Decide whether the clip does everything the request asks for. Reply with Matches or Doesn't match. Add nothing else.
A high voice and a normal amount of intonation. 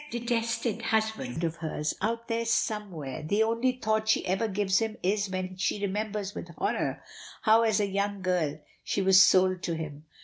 Matches